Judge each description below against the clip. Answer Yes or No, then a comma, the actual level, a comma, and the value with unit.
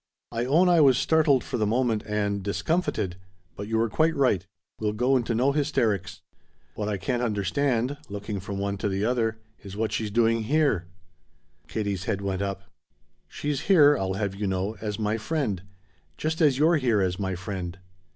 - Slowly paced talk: No, average, 180 wpm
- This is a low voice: Yes, low, 110 Hz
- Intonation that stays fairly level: No, average, 5.0 semitones